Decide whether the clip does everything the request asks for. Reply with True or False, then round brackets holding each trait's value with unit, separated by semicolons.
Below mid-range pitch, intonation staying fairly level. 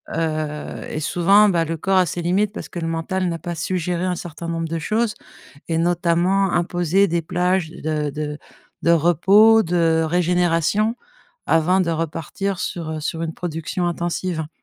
False (170 Hz; 2.1 semitones)